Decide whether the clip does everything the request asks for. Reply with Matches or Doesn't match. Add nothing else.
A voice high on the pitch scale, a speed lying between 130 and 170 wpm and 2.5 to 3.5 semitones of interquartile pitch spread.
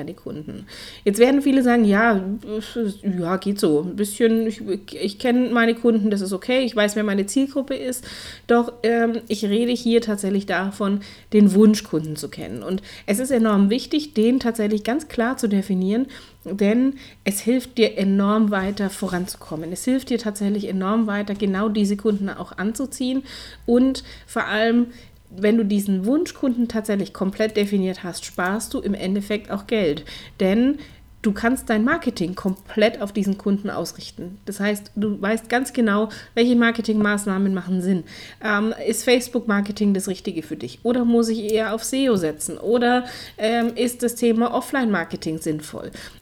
Matches